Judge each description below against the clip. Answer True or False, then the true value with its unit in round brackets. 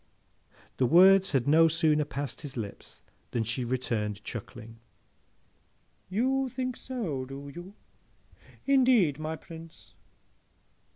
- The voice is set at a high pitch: False (155 Hz)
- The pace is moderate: False (110 wpm)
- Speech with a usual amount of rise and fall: False (7.1 semitones)